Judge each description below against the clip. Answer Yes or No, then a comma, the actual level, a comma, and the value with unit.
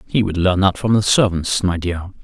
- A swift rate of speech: Yes, fast, 240 wpm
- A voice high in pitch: No, very low, 95 Hz